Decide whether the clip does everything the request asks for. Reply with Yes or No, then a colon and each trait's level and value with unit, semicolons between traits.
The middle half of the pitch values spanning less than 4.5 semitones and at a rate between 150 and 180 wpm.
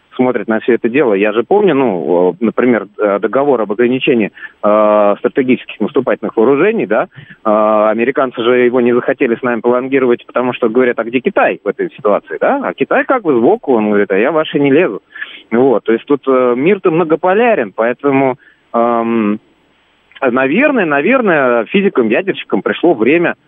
Yes: average, 2.9 semitones; fast, 160 wpm